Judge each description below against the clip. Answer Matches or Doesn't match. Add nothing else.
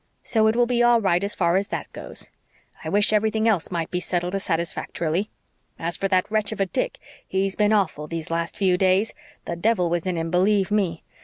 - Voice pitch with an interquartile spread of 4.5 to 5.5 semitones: Doesn't match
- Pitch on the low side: Doesn't match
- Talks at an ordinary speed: Doesn't match